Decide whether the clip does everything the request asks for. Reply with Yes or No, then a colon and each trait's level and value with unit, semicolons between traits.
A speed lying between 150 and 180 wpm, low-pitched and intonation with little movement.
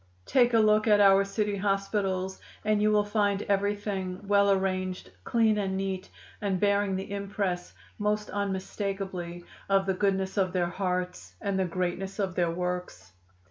No: average, 155 wpm; high, 195 Hz; narrow, 1.7 semitones